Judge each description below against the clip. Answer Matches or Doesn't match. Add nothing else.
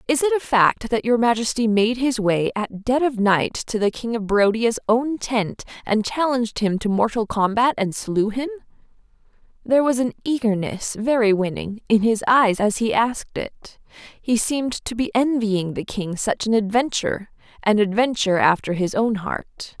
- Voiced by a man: Doesn't match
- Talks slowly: Doesn't match